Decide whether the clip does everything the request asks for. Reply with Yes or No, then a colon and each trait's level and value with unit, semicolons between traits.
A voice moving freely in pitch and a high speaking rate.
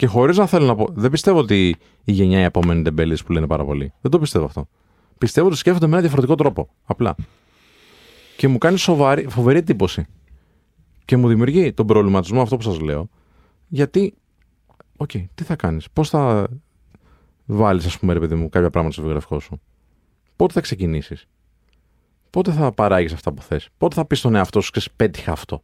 Yes: wide, 8.8 semitones; fast, 190 wpm